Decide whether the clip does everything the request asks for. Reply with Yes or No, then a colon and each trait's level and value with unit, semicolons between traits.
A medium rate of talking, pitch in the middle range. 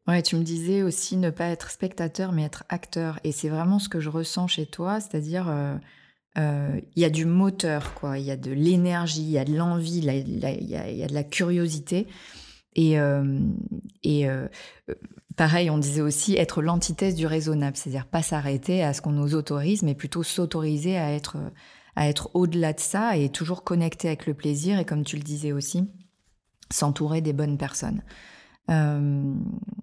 Yes: average, 190 wpm; medium, 160 Hz